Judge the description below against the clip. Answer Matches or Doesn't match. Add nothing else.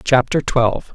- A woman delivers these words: Doesn't match